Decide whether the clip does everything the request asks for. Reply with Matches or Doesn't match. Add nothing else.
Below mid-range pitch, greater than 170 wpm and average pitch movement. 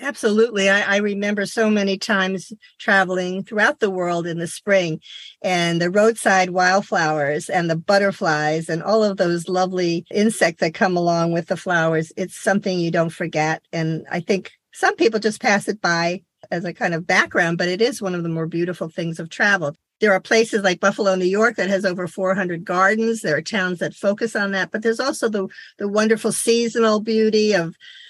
Doesn't match